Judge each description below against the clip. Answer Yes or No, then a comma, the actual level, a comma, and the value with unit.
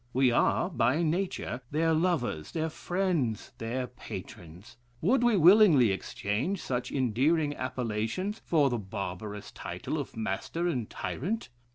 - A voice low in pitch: Yes, low, 130 Hz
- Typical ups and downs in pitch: No, wide, 7.2 semitones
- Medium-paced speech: No, slow, 130 wpm